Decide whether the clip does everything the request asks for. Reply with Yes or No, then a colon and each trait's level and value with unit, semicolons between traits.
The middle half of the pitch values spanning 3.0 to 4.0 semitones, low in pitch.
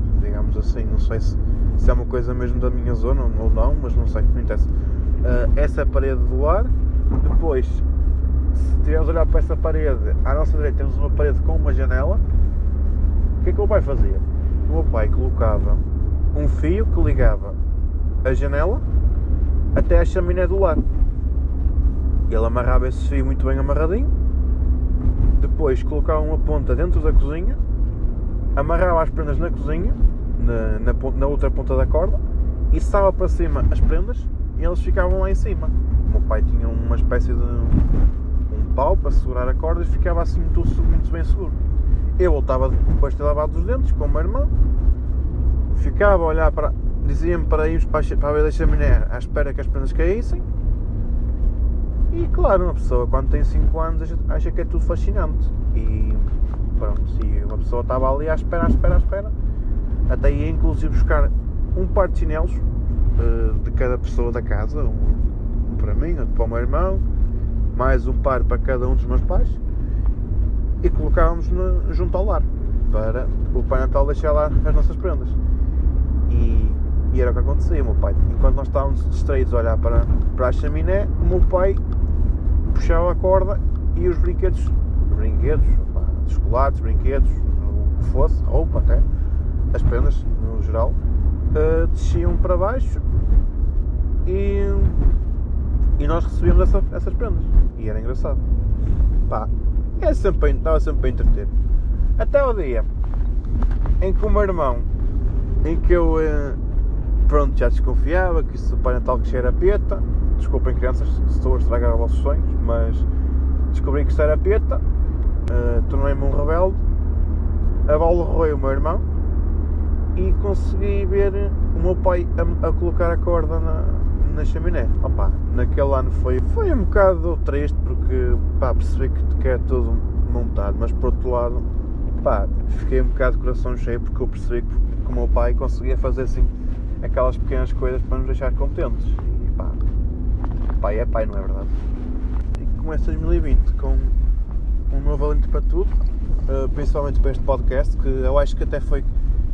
Yes: average, 3.6 semitones; very low, 70 Hz